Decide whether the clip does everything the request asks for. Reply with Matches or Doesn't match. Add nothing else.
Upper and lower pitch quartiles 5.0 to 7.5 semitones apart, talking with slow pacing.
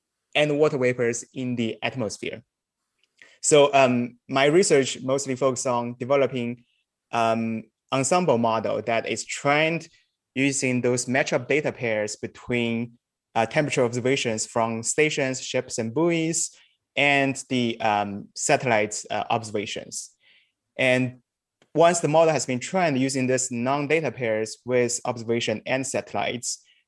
Doesn't match